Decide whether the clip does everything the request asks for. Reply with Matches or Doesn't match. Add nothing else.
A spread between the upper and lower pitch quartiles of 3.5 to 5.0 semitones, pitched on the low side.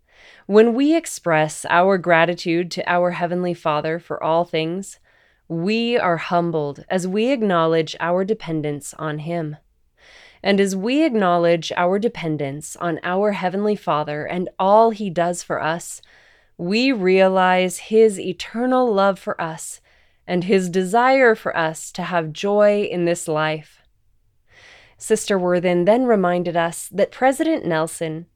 Doesn't match